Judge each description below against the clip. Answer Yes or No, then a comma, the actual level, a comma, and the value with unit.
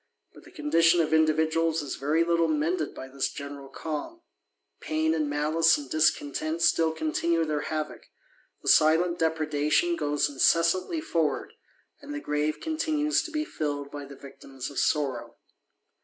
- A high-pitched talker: No, medium, 155 Hz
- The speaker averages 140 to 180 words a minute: Yes, average, 150 wpm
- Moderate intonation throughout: No, narrow, 2.3 semitones